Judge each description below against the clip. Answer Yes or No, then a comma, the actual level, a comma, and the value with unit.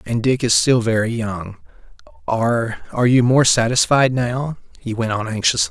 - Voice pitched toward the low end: Yes, low, 115 Hz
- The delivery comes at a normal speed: Yes, average, 160 wpm